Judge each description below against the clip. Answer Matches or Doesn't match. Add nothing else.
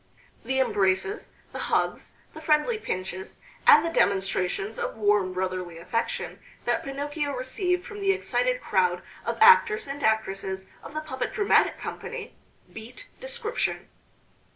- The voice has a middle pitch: Doesn't match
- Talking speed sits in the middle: Doesn't match